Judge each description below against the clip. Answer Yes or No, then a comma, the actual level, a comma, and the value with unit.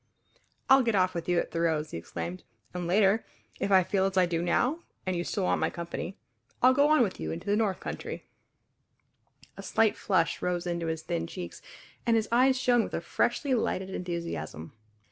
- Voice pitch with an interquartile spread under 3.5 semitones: No, average, 4.8 semitones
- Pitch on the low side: No, medium, 185 Hz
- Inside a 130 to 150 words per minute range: No, average, 200 wpm